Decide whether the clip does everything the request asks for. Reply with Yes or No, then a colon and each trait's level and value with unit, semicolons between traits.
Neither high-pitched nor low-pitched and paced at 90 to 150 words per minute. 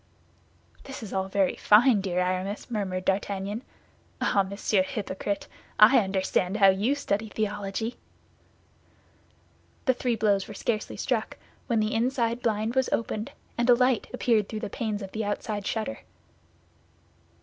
No: high, 210 Hz; average, 140 wpm